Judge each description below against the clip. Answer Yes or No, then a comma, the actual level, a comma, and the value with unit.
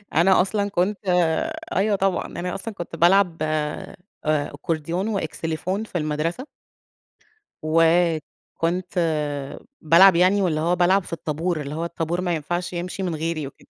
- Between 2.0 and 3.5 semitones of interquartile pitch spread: Yes, average, 2.9 semitones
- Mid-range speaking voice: Yes, medium, 175 Hz